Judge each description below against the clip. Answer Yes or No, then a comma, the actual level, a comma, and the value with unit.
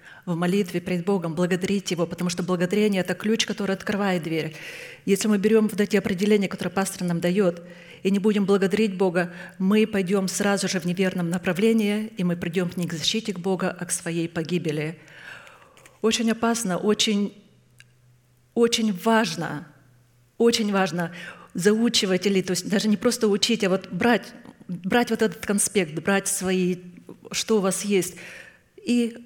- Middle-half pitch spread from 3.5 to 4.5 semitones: No, average, 3.0 semitones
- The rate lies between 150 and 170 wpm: Yes, fast, 160 wpm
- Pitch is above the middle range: Yes, high, 195 Hz